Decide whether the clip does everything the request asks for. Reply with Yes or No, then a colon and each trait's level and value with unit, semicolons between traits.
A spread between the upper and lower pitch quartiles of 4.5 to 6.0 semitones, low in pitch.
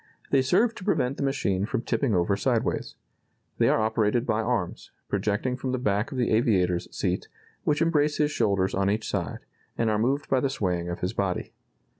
Yes: average, 5.2 semitones; low, 110 Hz